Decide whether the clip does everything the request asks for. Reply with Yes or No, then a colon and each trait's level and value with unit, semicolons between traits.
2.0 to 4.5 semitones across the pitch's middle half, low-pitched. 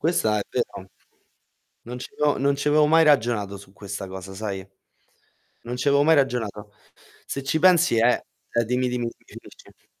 No: wide, 5.5 semitones; low, 125 Hz